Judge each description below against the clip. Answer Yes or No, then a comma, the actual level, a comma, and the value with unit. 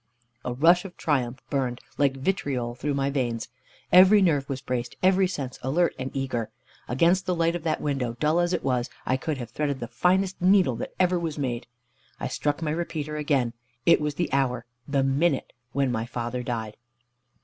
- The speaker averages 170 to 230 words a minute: Yes, average, 190 wpm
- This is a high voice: No, medium, 140 Hz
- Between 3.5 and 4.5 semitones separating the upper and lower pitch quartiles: No, average, 5.2 semitones